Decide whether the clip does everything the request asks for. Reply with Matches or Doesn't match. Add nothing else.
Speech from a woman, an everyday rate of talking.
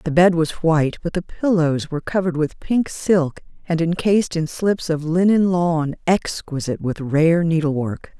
Matches